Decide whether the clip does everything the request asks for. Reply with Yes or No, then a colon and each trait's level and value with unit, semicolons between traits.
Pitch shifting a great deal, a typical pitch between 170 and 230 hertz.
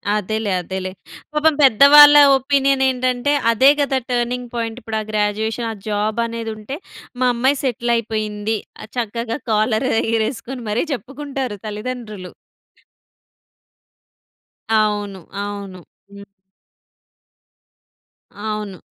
No: average, 3.3 semitones; high, 225 Hz